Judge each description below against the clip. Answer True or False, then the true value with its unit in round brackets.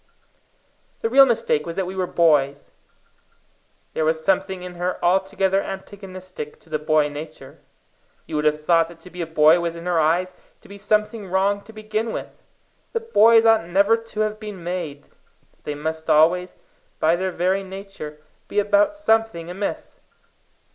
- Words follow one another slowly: False (170 wpm)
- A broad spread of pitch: False (4.0 semitones)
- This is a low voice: False (185 Hz)